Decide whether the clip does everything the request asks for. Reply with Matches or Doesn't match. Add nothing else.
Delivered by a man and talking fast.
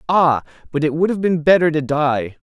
Matches